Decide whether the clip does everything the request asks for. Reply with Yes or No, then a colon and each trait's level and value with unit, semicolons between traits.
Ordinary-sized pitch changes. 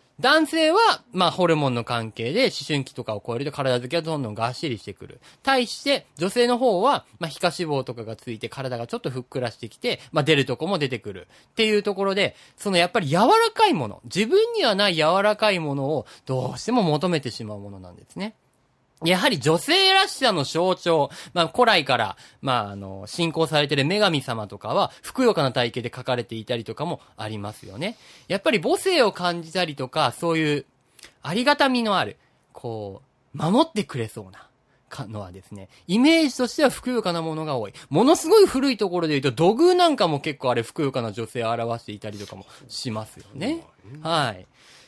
No: wide, 9.0 semitones